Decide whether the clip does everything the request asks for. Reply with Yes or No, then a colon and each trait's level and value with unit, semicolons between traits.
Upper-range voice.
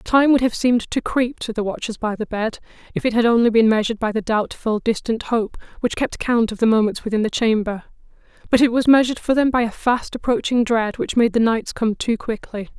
Yes: high, 230 Hz